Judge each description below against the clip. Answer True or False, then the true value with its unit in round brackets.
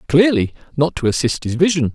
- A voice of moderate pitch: True (150 Hz)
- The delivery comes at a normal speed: True (185 wpm)